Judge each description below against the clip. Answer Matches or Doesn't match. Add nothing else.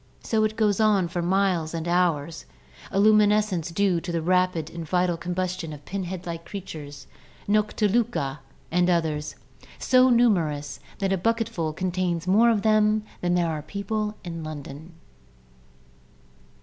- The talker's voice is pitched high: Doesn't match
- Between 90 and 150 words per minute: Matches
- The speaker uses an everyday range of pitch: Matches